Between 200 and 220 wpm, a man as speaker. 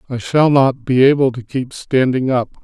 Yes: fast, 205 wpm; male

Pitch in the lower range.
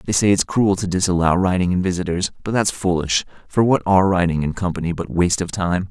Yes: very low, 90 Hz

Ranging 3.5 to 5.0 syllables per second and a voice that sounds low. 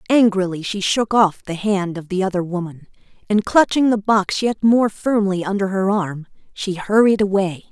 No: 4.8 syllables/s; high, 195 Hz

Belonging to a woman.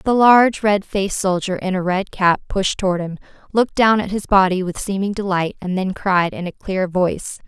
Yes: female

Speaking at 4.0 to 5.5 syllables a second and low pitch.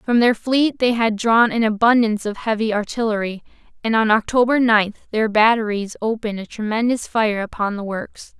No: 5.1 syllables/s; high, 220 Hz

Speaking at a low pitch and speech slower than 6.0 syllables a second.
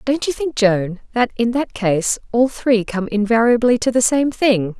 No: high, 230 Hz; 4.4 syllables/s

